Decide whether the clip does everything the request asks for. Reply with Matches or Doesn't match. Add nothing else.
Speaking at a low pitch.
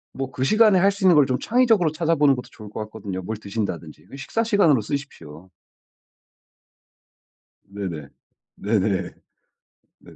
Matches